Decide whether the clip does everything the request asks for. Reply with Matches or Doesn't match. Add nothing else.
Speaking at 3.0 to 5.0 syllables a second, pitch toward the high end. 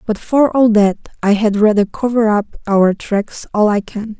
Matches